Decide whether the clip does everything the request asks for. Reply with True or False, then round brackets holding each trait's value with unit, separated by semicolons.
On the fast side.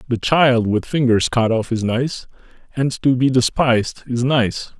False (175 wpm)